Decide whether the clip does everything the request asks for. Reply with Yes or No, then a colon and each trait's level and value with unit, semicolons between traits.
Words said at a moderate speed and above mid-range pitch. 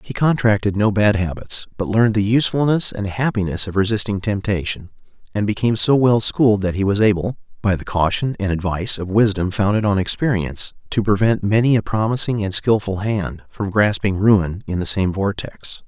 No: average, 180 wpm; low, 105 Hz